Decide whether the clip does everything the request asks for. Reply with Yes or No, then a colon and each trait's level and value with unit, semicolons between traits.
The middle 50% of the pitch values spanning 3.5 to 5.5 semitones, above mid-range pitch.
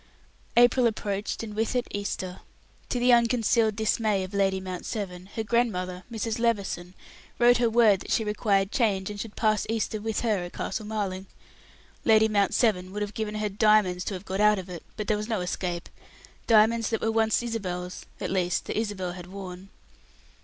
No: average, 2.9 semitones; high, 210 Hz